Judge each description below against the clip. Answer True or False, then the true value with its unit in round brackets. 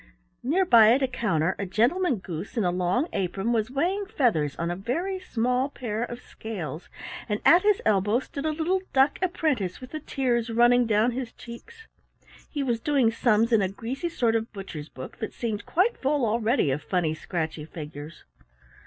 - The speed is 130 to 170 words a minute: False (185 wpm)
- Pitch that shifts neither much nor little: False (6.3 semitones)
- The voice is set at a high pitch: True (235 Hz)